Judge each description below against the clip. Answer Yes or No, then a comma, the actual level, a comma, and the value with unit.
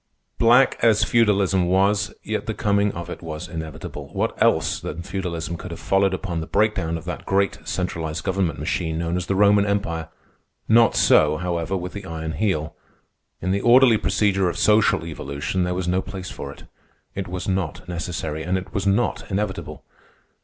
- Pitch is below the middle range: Yes, very low, 95 Hz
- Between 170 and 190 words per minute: Yes, average, 180 wpm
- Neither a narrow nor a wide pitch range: Yes, average, 3.3 semitones